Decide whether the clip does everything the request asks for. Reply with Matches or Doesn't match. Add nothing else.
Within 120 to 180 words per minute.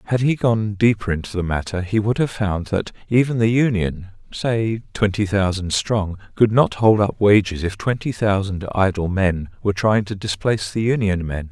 Doesn't match